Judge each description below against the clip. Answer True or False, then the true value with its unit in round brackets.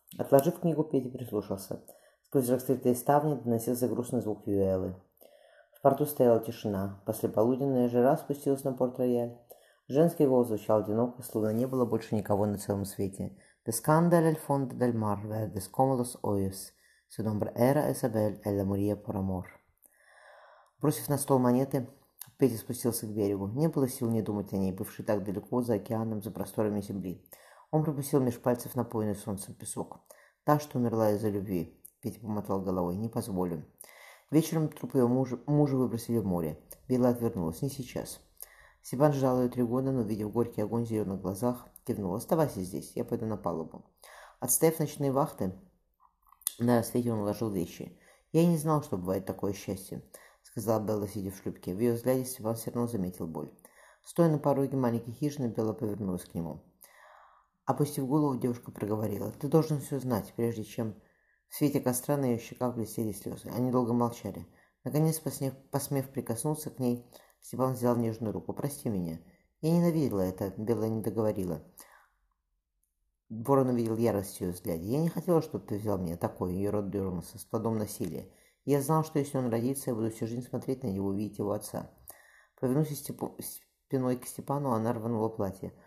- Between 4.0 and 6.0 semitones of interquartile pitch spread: True (4.6 semitones)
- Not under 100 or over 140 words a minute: False (160 wpm)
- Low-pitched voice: True (115 Hz)